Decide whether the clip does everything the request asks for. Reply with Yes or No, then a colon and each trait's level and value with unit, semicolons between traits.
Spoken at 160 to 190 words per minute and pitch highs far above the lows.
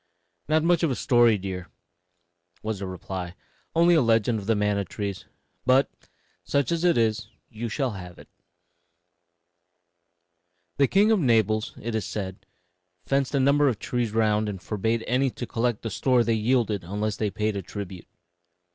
No: average, 170 wpm; average, 4.1 semitones